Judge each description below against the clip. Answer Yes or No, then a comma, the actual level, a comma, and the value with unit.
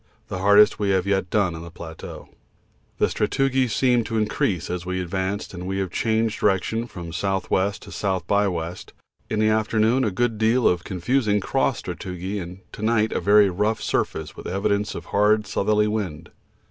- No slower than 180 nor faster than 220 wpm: Yes, average, 185 wpm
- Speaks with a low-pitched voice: Yes, low, 100 Hz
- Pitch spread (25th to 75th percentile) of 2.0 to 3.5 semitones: Yes, average, 2.9 semitones